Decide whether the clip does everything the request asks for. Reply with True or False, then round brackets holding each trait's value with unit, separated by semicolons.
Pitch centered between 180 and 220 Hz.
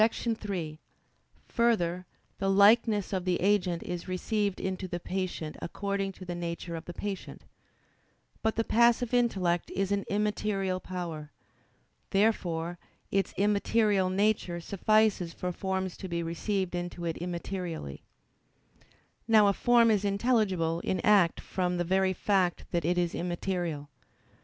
True (190 Hz)